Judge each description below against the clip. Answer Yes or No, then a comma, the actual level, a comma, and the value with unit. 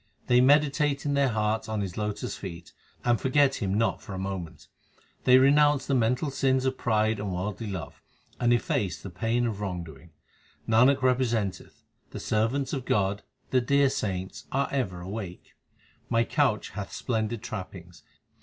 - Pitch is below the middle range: Yes, low, 110 Hz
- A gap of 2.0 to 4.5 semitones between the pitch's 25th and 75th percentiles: No, average, 5.1 semitones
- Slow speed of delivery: No, average, 165 wpm